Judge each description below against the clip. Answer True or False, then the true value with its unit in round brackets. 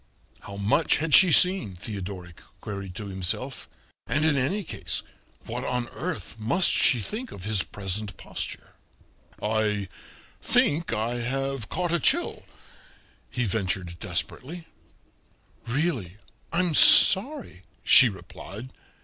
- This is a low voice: True (115 Hz)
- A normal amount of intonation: False (8.2 semitones)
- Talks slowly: True (120 wpm)